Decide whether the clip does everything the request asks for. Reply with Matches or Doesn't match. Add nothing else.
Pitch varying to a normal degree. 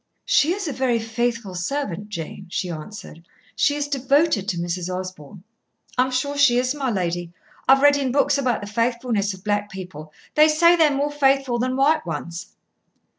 Doesn't match